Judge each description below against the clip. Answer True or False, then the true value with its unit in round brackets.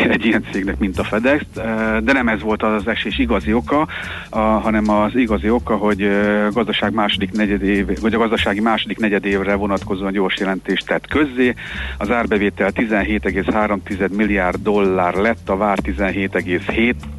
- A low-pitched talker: True (105 Hz)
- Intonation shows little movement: True (1.8 semitones)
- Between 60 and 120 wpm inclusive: False (150 wpm)